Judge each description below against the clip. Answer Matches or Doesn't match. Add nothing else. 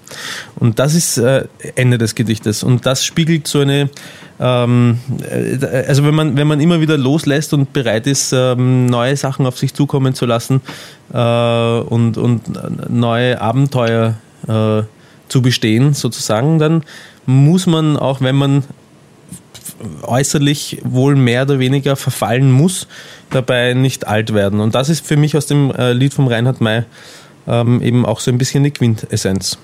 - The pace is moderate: Matches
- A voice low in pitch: Matches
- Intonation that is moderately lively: Matches